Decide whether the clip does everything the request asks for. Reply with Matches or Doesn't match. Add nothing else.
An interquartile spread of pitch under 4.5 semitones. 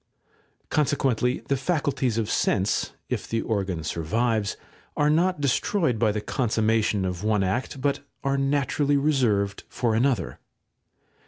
Doesn't match